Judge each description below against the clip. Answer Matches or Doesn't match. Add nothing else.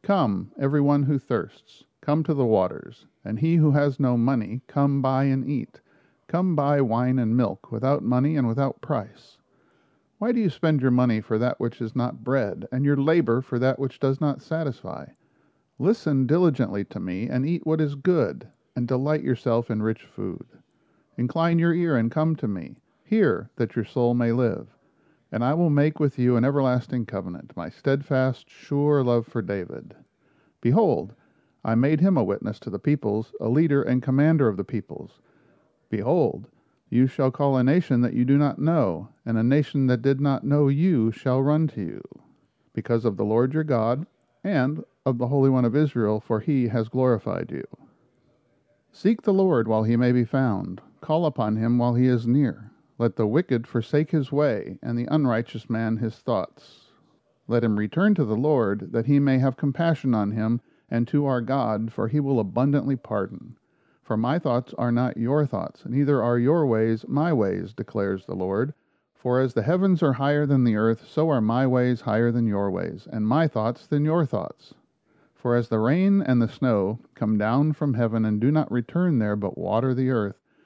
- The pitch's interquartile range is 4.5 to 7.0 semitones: Doesn't match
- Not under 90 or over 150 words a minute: Doesn't match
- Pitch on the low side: Matches